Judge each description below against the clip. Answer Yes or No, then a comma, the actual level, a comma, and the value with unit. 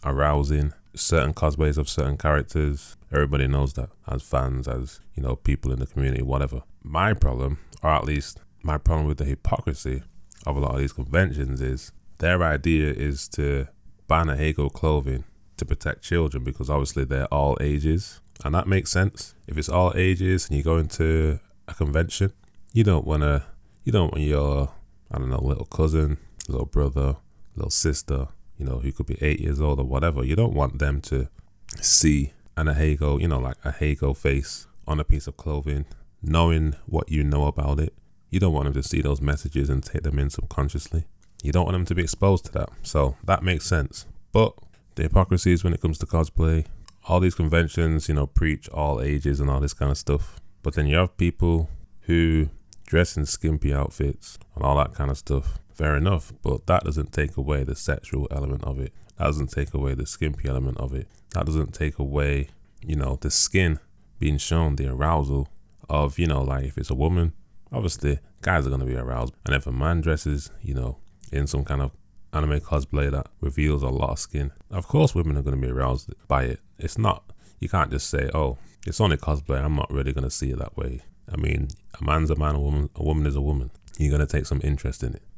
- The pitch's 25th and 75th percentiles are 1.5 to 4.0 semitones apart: Yes, average, 3.7 semitones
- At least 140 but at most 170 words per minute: No, fast, 205 wpm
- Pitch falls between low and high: No, very low, 75 Hz